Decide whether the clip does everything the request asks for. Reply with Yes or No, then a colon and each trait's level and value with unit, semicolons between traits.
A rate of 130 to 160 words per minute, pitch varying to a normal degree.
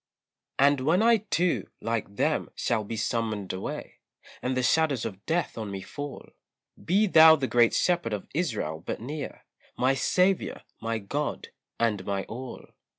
No: average, 155 wpm; wide, 6.6 semitones